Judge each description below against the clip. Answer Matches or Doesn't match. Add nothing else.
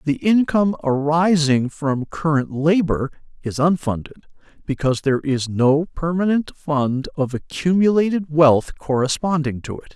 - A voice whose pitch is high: Doesn't match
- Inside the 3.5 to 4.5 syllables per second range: Doesn't match